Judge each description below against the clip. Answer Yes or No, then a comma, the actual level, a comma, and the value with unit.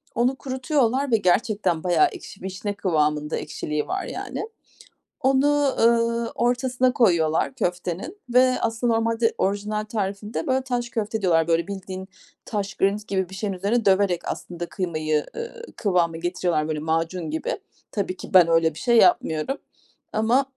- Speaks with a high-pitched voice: Yes, high, 200 Hz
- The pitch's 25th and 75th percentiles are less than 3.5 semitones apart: No, wide, 5.4 semitones